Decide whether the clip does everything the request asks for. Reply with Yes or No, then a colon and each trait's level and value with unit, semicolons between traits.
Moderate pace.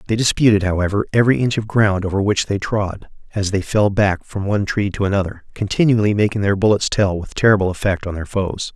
No: fast, 210 wpm